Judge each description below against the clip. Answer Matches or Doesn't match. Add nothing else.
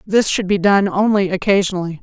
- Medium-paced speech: Matches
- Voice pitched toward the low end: Doesn't match